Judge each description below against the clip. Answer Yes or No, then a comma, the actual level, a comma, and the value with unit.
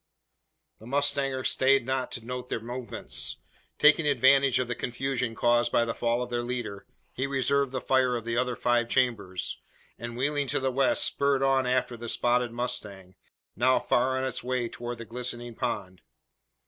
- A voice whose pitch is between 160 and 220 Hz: No, low, 125 Hz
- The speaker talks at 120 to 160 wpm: No, average, 175 wpm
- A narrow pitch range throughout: Yes, narrow, 1.9 semitones